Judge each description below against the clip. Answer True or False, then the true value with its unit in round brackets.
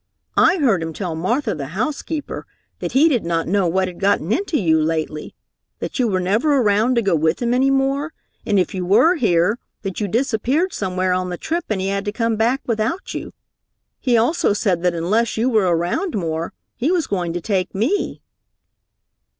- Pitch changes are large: True (6.0 semitones)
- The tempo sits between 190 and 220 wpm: True (200 wpm)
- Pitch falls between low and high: False (205 Hz)